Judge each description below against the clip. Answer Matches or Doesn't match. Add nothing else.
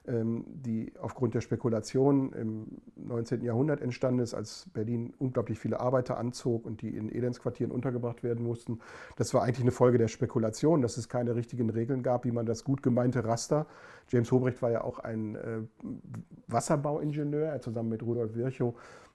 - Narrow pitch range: Matches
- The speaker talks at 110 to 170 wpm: Matches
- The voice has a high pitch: Doesn't match